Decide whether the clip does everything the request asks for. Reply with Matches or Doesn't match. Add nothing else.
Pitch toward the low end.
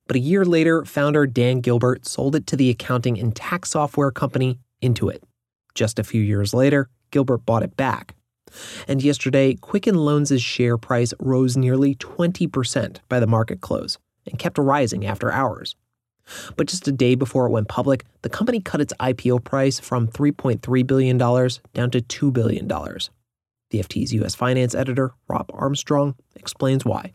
Matches